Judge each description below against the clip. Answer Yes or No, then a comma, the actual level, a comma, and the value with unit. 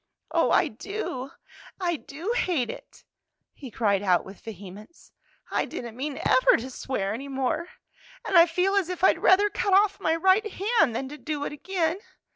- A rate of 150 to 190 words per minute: Yes, average, 180 wpm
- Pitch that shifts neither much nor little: No, wide, 7.2 semitones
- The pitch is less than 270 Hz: No, very high, 320 Hz